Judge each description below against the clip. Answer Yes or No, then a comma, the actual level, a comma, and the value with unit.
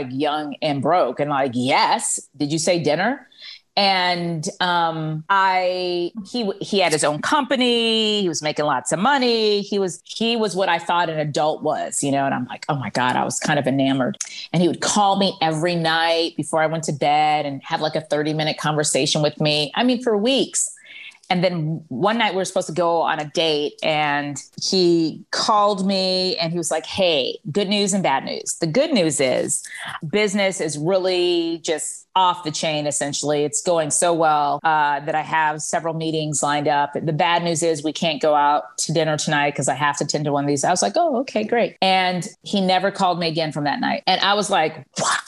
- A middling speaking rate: No, fast, 215 wpm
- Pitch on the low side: No, medium, 165 Hz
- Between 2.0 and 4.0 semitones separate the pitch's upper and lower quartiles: No, average, 4.4 semitones